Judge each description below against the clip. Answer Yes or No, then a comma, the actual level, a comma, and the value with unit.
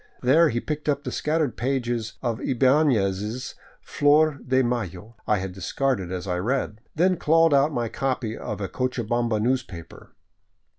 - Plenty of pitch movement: No, average, 4.7 semitones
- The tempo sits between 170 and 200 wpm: No, average, 160 wpm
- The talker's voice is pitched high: No, low, 125 Hz